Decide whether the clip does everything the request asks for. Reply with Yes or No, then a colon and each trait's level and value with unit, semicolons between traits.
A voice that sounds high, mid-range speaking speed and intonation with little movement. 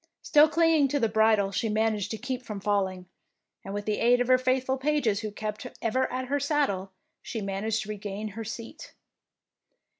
No: high, 225 Hz; average, 185 wpm; average, 3.9 semitones